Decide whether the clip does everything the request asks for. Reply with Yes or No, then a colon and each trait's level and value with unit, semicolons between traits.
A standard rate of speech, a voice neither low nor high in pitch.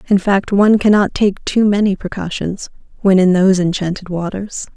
No: average, 165 wpm; high, 195 Hz